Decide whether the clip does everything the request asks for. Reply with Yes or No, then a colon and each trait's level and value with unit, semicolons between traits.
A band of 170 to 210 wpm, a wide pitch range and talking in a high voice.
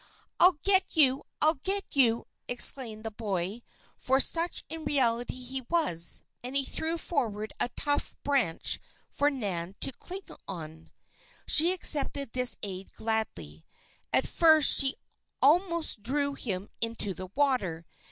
No: slow, 135 wpm; wide, 6.2 semitones; very high, 255 Hz